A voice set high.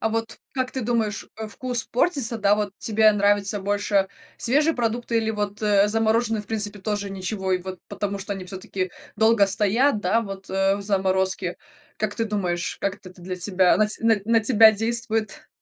Yes: high, 210 Hz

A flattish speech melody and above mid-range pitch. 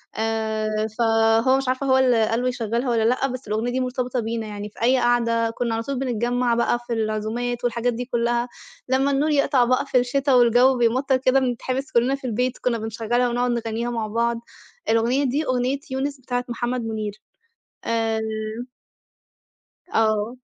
Yes: narrow, 2.2 semitones; high, 240 Hz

